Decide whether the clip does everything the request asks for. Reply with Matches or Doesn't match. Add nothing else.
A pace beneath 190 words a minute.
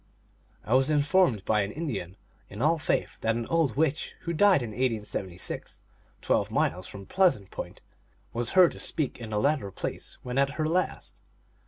Matches